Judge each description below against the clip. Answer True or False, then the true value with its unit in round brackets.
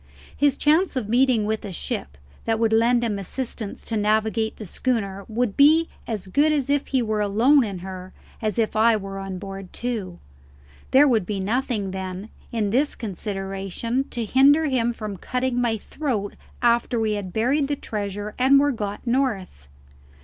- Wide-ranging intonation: False (4.3 semitones)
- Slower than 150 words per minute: False (170 wpm)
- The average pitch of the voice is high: True (220 Hz)